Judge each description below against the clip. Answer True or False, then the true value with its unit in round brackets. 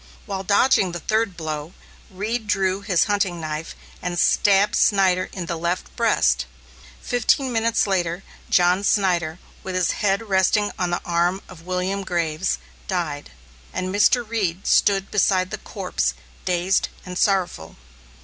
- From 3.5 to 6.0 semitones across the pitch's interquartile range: False (2.6 semitones)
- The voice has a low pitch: False (185 Hz)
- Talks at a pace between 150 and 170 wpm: False (140 wpm)